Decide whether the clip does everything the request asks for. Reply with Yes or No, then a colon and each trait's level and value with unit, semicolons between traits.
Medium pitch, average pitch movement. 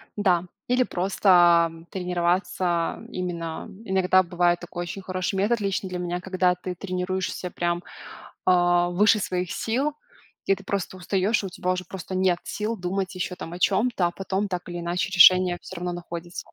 No: medium, 180 Hz; narrow, 1.6 semitones